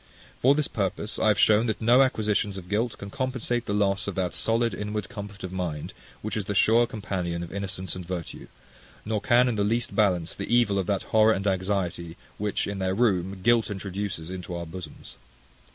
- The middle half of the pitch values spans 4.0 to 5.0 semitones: No, average, 2.9 semitones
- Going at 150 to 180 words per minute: No, average, 200 wpm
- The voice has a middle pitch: No, low, 100 Hz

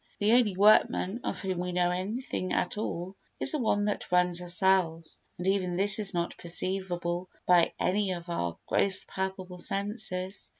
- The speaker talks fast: No, average, 165 wpm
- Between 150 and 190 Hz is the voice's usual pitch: Yes, medium, 185 Hz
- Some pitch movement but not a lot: No, narrow, 2.2 semitones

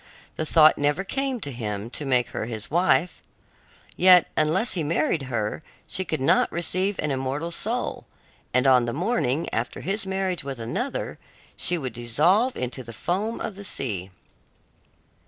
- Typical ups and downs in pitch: No, wide, 6.9 semitones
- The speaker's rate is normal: Yes, average, 160 wpm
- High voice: No, medium, 150 Hz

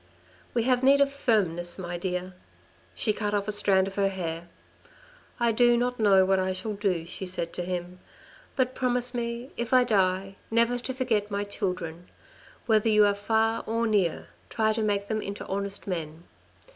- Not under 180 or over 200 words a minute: Yes, average, 190 wpm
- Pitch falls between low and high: No, high, 205 Hz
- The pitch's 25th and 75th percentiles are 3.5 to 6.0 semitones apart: Yes, average, 3.9 semitones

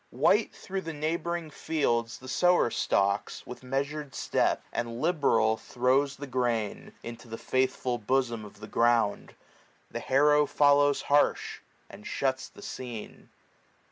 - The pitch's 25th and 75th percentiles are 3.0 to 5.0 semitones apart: Yes, average, 4.0 semitones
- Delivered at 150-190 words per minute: No, average, 140 wpm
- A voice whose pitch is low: Yes, low, 130 Hz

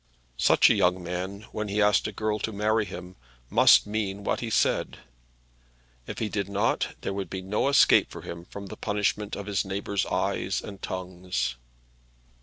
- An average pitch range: No, narrow, 2.1 semitones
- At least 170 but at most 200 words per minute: Yes, average, 180 wpm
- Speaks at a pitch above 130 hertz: No, low, 100 Hz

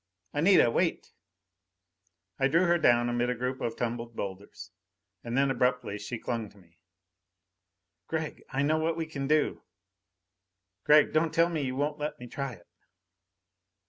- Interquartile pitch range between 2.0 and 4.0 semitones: No, average, 4.5 semitones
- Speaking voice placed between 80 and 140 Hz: Yes, low, 135 Hz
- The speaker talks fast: No, average, 155 wpm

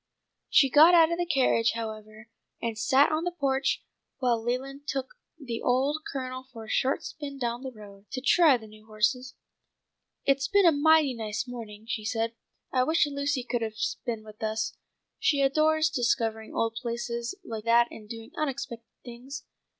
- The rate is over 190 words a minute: No, average, 175 wpm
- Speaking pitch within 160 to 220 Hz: No, very high, 250 Hz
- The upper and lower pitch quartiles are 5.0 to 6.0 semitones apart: No, average, 3.7 semitones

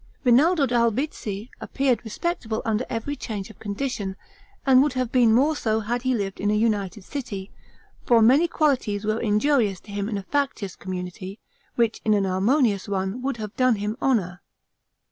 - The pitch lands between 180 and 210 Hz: No, high, 225 Hz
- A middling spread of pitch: Yes, average, 4.1 semitones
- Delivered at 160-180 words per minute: Yes, average, 170 wpm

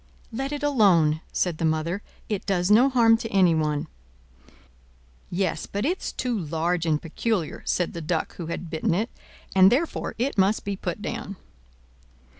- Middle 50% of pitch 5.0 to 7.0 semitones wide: Yes, wide, 5.4 semitones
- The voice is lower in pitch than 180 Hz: No, high, 190 Hz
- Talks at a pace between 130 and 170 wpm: Yes, average, 160 wpm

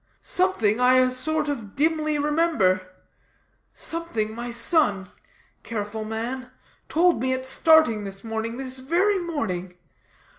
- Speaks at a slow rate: Yes, slow, 120 wpm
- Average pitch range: No, wide, 6.3 semitones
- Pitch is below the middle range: No, very high, 255 Hz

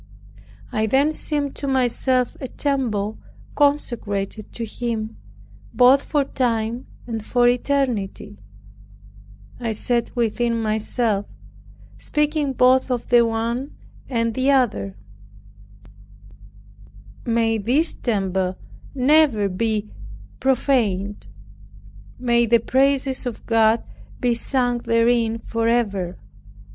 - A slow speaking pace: Yes, slow, 95 wpm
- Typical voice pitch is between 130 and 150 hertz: No, high, 235 Hz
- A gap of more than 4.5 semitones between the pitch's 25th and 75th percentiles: No, average, 3.1 semitones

